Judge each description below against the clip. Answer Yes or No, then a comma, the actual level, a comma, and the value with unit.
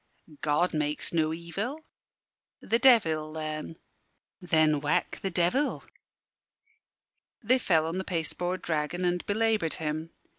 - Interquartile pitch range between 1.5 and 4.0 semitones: Yes, average, 3.4 semitones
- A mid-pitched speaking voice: Yes, medium, 165 Hz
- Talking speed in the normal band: No, slow, 115 wpm